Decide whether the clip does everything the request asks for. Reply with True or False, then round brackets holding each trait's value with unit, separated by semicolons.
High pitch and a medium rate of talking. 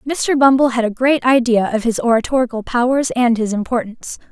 True (245 Hz; 180 wpm)